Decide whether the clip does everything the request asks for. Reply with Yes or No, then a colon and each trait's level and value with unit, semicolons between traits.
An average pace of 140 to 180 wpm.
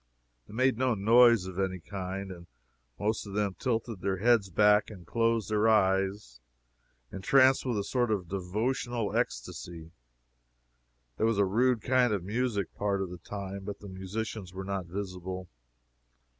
Yes: average, 155 wpm